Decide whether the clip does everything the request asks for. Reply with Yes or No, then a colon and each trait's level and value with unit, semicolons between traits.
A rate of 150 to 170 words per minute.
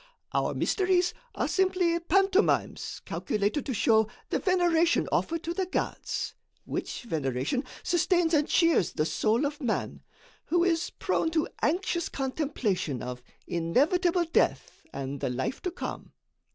No: slow, 135 wpm